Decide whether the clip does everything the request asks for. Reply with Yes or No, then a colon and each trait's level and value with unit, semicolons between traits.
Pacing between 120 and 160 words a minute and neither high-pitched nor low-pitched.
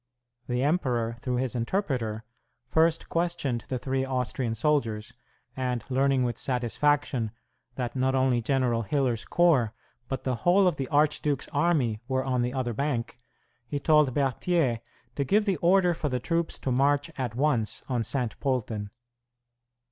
No: average, 150 wpm; low, 130 Hz